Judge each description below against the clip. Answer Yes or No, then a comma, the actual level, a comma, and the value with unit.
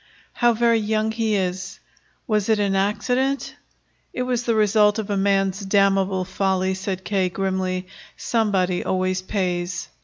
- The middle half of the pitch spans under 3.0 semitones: Yes, narrow, 2.5 semitones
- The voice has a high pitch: Yes, high, 195 Hz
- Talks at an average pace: Yes, average, 145 wpm